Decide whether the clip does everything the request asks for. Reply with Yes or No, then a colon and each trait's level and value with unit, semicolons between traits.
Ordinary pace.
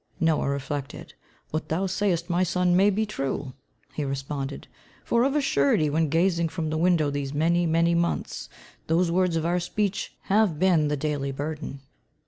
Yes: average, 170 wpm